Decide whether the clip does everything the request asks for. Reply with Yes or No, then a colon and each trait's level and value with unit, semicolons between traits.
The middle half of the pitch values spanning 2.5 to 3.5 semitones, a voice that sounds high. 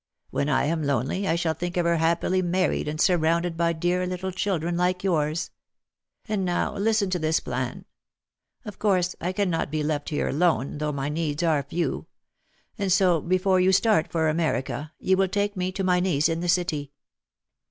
No: average, 2.9 semitones; medium, 175 Hz